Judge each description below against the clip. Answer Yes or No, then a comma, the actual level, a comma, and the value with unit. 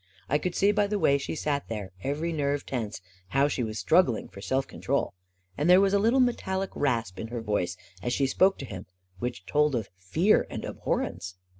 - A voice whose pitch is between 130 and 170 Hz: Yes, medium, 140 Hz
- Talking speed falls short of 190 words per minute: No, fast, 205 wpm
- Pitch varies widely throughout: Yes, wide, 8.1 semitones